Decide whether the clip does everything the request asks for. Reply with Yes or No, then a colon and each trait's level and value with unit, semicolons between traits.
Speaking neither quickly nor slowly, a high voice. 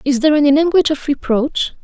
Yes: average, 195 wpm; very high, 285 Hz